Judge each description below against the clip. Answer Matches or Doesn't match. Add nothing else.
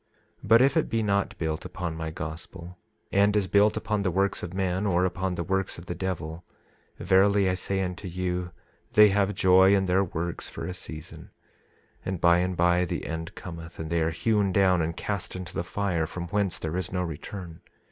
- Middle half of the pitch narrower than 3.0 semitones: Matches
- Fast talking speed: Matches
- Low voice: Matches